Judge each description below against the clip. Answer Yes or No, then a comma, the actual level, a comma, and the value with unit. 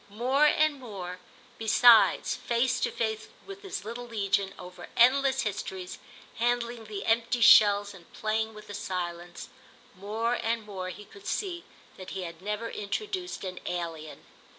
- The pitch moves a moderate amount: Yes, average, 4.2 semitones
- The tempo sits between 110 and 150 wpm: Yes, average, 145 wpm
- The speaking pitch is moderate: No, high, 220 Hz